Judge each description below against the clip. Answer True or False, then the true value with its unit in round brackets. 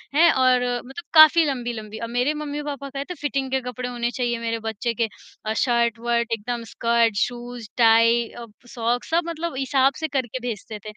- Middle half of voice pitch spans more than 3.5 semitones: False (2.9 semitones)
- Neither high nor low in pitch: False (245 Hz)